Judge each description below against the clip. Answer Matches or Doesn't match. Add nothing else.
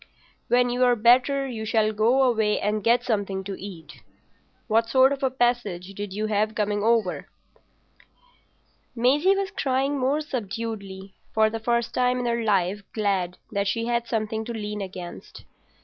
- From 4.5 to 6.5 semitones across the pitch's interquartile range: Doesn't match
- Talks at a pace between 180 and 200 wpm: Doesn't match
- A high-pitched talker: Matches